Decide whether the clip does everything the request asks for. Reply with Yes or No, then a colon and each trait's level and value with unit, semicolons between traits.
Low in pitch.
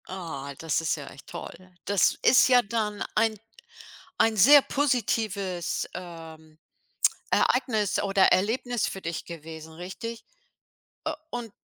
No: high, 195 Hz